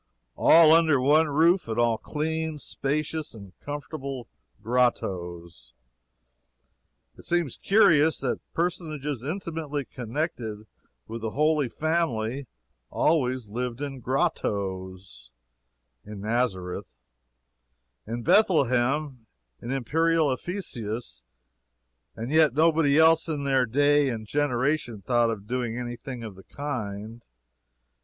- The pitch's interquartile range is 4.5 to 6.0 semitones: Yes, wide, 5.4 semitones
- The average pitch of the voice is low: Yes, low, 130 Hz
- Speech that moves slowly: Yes, slow, 105 wpm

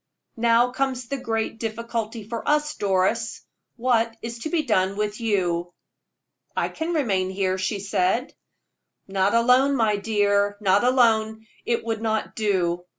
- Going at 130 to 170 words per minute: Yes, average, 145 wpm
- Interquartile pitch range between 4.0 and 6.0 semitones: No, average, 2.9 semitones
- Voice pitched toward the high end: Yes, high, 220 Hz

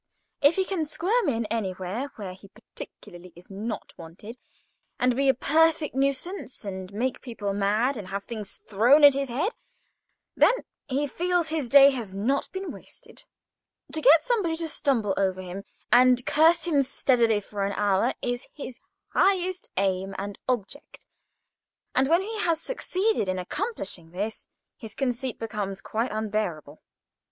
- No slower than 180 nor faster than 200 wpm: No, average, 155 wpm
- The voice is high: Yes, high, 245 Hz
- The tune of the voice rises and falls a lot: Yes, wide, 7.4 semitones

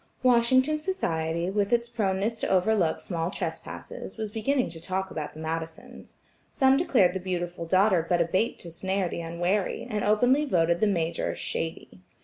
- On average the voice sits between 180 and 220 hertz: Yes, high, 190 Hz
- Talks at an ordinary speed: Yes, average, 160 wpm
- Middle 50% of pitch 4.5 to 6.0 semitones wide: Yes, average, 5.1 semitones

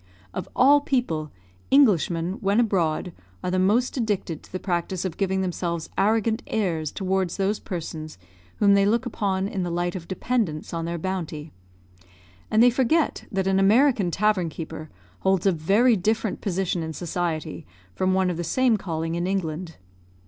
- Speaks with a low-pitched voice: No, high, 190 Hz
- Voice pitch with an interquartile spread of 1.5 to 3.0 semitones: No, average, 3.9 semitones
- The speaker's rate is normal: Yes, average, 165 wpm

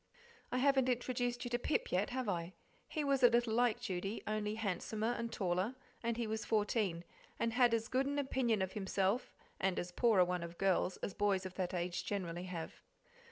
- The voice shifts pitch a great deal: No, average, 4.6 semitones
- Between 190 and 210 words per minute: Yes, fast, 205 wpm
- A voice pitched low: No, high, 215 Hz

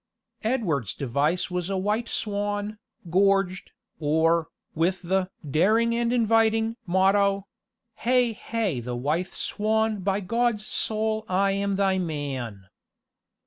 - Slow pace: Yes, slow, 115 wpm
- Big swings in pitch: No, average, 4.5 semitones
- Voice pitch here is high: Yes, high, 195 Hz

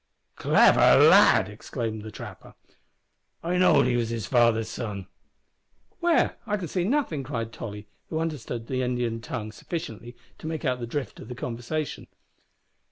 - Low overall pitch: Yes, low, 120 Hz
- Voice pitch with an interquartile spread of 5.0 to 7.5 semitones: Yes, wide, 5.5 semitones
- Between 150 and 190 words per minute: Yes, average, 155 wpm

